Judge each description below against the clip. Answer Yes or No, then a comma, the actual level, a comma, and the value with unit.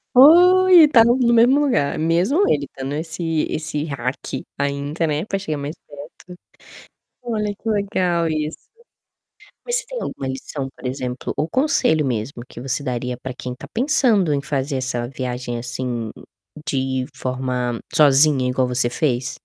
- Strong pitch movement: Yes, wide, 7.0 semitones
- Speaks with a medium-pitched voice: Yes, medium, 145 Hz